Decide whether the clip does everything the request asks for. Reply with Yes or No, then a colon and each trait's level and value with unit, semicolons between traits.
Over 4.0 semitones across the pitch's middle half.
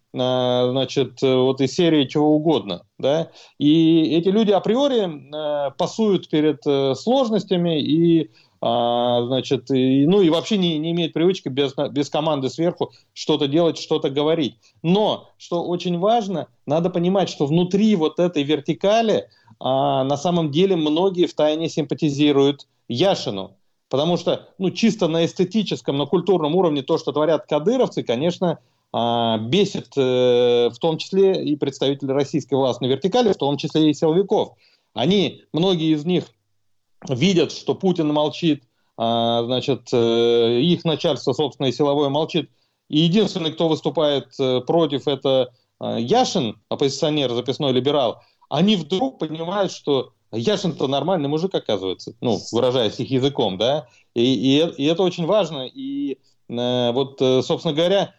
Yes: average, 4.6 semitones